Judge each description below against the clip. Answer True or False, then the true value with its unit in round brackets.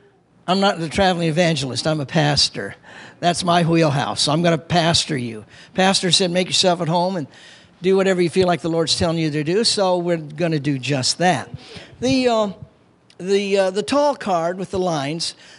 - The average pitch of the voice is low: False (170 Hz)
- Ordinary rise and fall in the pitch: True (3.5 semitones)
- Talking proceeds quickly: False (195 wpm)